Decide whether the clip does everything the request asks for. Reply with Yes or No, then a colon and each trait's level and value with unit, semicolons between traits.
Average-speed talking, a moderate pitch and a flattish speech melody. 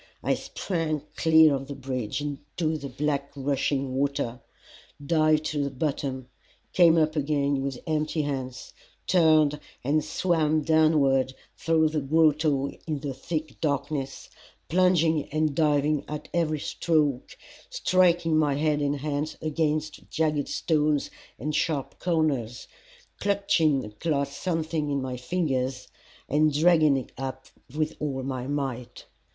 No: slow, 130 wpm; medium, 150 Hz; narrow, 2.3 semitones